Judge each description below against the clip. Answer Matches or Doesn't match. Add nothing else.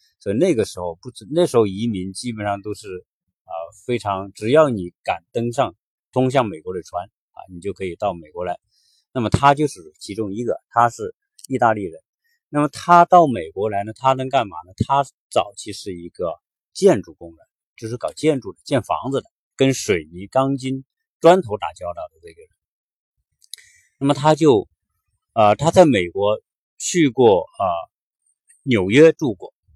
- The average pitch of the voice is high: Doesn't match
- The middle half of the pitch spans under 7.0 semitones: Doesn't match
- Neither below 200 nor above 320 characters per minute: Matches